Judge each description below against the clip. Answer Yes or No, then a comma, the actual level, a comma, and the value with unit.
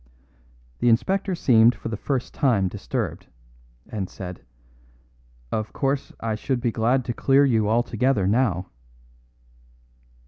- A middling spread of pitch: Yes, average, 4.1 semitones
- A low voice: Yes, low, 115 Hz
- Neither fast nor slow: No, slow, 125 wpm